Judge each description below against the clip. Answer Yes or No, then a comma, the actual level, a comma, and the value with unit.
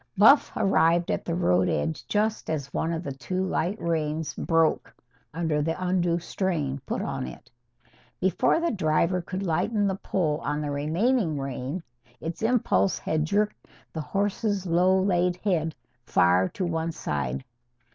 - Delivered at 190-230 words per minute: No, average, 155 wpm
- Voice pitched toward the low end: No, medium, 170 Hz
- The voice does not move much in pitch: No, average, 3.7 semitones